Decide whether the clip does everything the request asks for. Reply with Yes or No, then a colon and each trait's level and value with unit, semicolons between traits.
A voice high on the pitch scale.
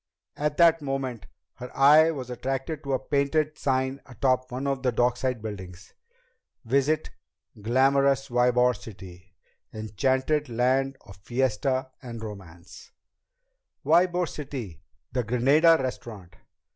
No: low, 130 Hz